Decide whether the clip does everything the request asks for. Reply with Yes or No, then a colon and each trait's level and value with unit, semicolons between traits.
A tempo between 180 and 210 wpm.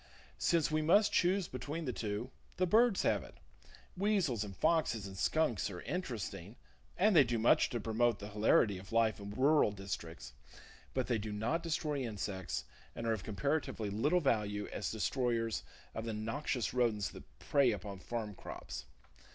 No: average, 170 wpm